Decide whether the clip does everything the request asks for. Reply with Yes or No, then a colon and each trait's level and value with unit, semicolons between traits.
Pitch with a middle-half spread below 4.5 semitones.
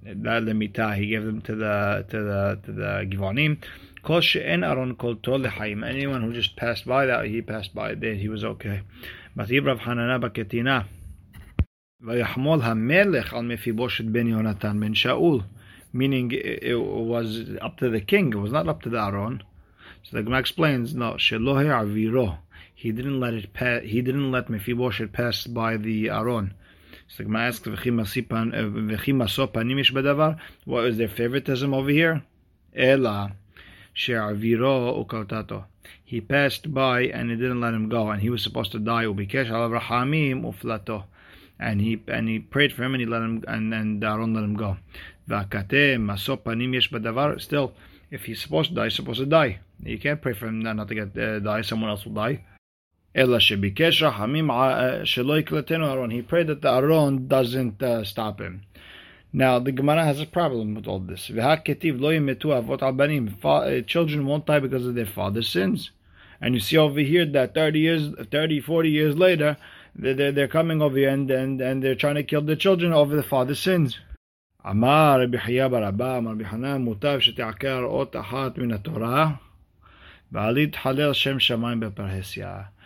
Yes: average, 4.1 semitones